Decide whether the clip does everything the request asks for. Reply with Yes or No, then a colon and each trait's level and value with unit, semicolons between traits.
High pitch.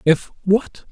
Yes: high, 195 Hz